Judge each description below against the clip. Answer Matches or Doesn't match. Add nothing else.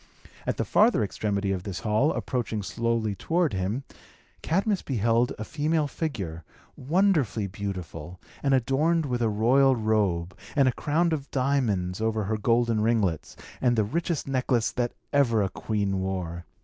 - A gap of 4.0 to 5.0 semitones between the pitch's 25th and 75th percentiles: Doesn't match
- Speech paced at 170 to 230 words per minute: Doesn't match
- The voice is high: Doesn't match